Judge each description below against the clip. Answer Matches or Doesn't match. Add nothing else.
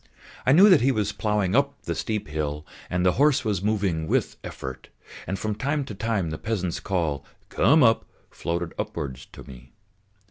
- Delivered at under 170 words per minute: Doesn't match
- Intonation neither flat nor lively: Doesn't match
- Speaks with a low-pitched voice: Matches